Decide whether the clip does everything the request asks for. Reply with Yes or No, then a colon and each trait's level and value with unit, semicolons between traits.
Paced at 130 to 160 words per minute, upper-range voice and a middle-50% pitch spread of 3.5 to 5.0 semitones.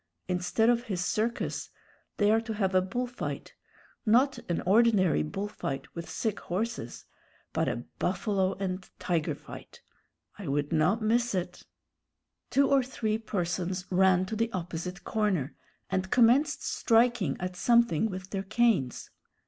Yes: average, 150 wpm; high, 195 Hz; average, 4.1 semitones